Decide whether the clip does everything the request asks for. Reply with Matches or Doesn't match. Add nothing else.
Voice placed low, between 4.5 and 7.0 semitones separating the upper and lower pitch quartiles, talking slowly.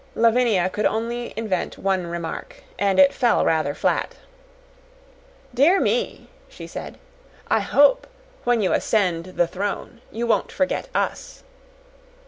Doesn't match